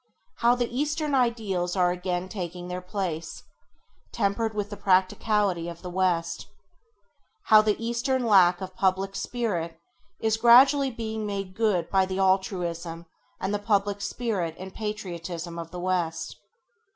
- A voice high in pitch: Yes, high, 195 Hz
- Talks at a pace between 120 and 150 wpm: Yes, average, 145 wpm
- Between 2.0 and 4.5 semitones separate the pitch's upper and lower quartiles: Yes, average, 3.7 semitones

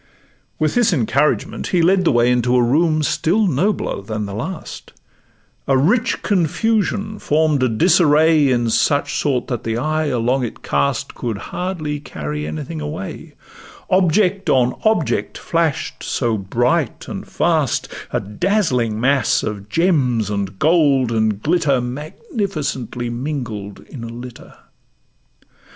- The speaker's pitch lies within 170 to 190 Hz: No, medium, 140 Hz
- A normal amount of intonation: No, wide, 6.2 semitones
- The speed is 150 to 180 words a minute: No, slow, 135 wpm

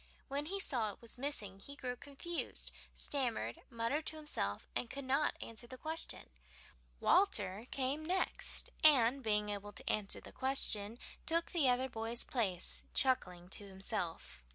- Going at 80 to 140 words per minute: No, average, 155 wpm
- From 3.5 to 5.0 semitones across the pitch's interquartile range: No, wide, 5.5 semitones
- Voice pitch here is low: No, high, 245 Hz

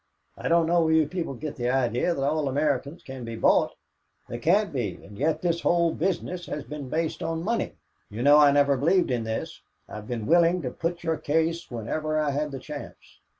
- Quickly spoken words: Yes, fast, 215 wpm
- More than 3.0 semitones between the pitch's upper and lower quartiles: Yes, average, 4.0 semitones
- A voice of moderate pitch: Yes, medium, 150 Hz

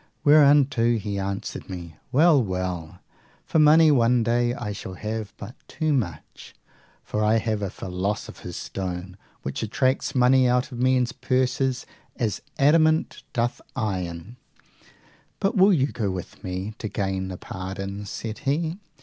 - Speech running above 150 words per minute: No, average, 145 wpm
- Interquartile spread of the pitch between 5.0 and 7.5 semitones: Yes, wide, 5.5 semitones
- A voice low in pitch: Yes, low, 115 Hz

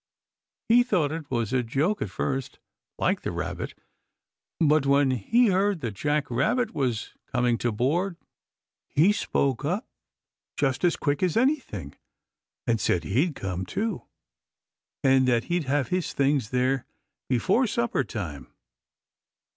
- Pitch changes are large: Yes, wide, 6.8 semitones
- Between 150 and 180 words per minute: No, average, 140 wpm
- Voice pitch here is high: No, medium, 140 Hz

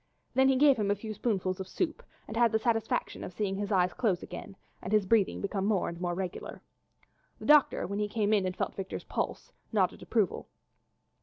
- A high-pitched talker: Yes, high, 205 Hz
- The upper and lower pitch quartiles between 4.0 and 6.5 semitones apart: No, average, 3.0 semitones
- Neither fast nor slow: No, fast, 210 wpm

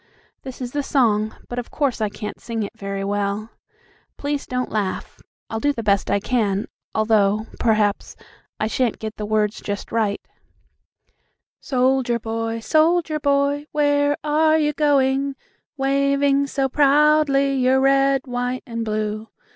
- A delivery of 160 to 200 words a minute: No, average, 145 wpm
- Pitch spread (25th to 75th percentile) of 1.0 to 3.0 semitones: No, average, 4.5 semitones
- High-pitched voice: Yes, very high, 250 Hz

